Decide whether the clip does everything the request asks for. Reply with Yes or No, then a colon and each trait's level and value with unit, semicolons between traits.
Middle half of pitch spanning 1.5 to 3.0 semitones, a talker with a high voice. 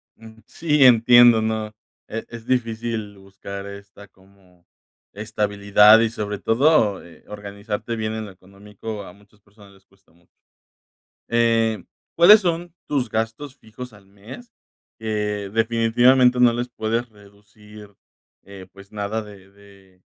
No: narrow, 2.5 semitones; low, 110 Hz